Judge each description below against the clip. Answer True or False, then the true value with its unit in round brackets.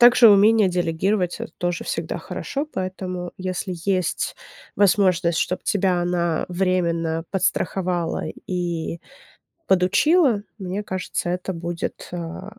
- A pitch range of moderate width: False (2.0 semitones)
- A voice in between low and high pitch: True (180 Hz)